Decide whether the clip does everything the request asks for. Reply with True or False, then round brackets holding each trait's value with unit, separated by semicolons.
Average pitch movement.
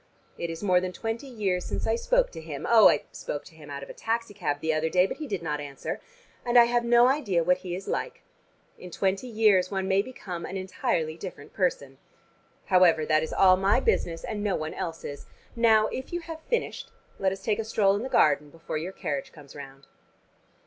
False (5.8 semitones)